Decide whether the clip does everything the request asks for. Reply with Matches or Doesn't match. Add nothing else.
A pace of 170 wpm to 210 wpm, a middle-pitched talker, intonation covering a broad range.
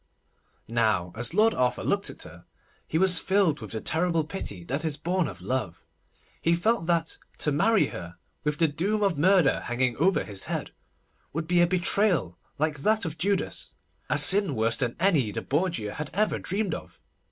Matches